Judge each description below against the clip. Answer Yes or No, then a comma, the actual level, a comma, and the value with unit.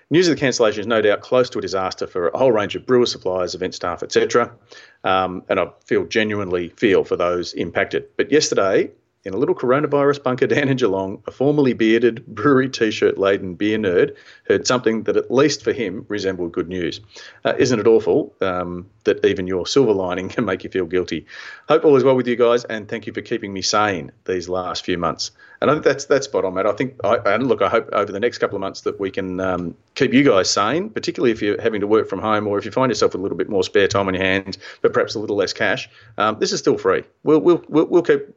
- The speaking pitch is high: No, low, 115 Hz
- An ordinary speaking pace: No, fast, 245 wpm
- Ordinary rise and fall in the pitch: No, wide, 7.5 semitones